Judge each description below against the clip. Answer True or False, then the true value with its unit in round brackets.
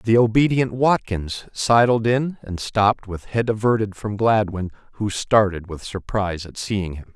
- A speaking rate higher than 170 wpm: False (160 wpm)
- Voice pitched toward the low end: True (105 Hz)